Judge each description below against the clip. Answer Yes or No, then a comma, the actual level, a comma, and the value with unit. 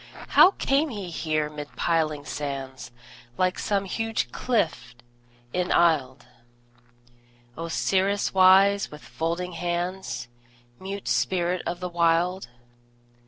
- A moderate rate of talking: No, slow, 100 wpm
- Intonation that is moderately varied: Yes, average, 3.7 semitones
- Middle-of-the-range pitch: Yes, medium, 175 Hz